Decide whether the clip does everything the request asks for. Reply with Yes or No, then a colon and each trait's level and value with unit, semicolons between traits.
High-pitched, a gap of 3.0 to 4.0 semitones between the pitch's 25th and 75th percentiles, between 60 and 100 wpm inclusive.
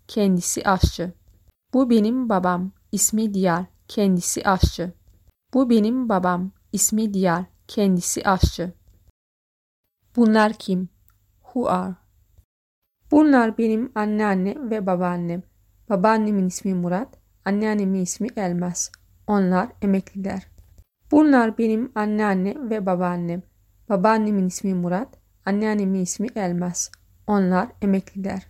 Yes: high, 195 Hz; average, 3.3 semitones; slow, 95 wpm